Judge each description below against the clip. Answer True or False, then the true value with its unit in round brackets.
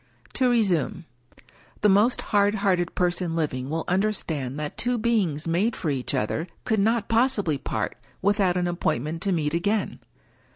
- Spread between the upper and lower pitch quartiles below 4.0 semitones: False (4.8 semitones)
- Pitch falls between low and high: True (180 Hz)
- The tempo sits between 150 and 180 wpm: True (155 wpm)